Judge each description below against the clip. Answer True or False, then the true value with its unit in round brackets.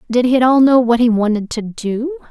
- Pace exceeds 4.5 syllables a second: True (5.5 syllables/s)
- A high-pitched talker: True (245 Hz)